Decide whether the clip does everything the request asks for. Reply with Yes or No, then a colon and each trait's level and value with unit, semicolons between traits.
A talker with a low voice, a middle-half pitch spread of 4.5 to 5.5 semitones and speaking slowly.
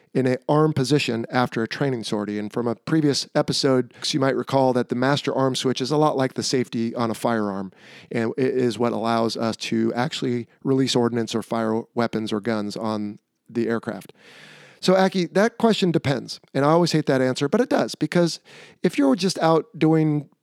No: low, 130 Hz; average, 4.8 semitones; average, 200 wpm